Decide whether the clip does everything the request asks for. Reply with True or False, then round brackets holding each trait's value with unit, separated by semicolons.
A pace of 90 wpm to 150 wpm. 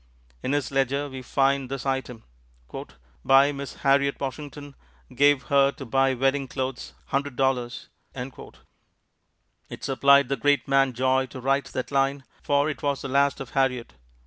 True (145 wpm)